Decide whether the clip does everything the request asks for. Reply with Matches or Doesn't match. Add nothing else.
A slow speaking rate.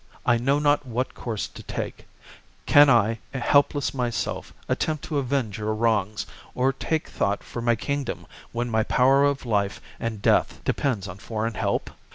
Doesn't match